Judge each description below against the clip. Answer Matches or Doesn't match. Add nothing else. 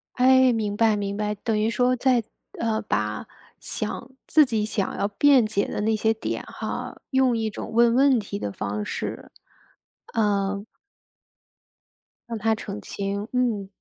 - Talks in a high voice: Matches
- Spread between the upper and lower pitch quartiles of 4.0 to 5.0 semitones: Doesn't match